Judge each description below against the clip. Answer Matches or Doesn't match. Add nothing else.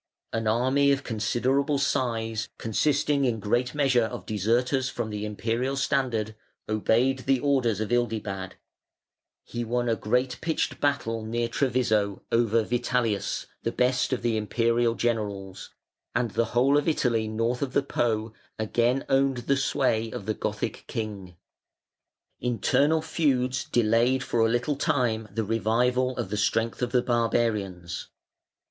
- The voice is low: Matches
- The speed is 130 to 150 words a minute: Matches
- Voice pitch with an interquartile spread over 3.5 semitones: Doesn't match